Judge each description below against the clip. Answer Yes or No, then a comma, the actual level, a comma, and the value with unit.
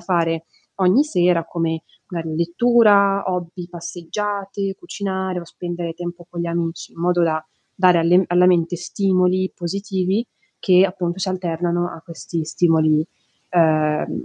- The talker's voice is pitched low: No, medium, 175 Hz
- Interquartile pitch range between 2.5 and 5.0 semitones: No, narrow, 2.0 semitones